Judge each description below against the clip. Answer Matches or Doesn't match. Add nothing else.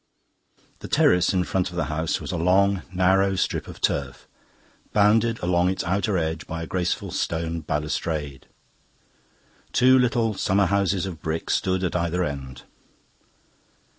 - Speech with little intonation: Doesn't match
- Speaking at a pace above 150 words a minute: Doesn't match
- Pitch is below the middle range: Matches